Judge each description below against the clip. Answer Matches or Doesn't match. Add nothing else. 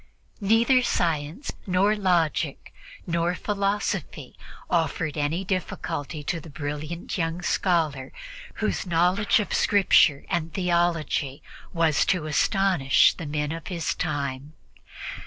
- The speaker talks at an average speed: Doesn't match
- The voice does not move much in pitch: Doesn't match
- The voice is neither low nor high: Matches